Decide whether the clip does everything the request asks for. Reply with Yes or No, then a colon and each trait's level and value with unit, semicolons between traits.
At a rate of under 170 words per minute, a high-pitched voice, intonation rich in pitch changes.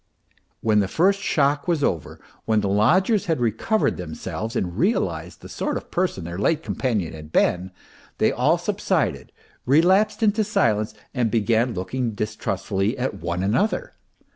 No: average, 150 wpm; low, 115 Hz; wide, 8.9 semitones